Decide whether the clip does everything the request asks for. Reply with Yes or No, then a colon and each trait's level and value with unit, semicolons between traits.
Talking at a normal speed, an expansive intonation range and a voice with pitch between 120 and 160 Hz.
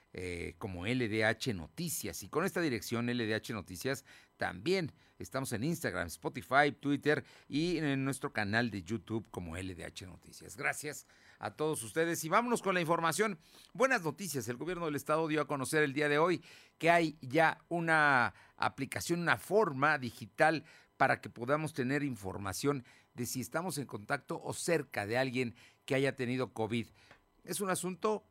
Yes: average, 160 wpm; wide, 5.9 semitones; low, 135 Hz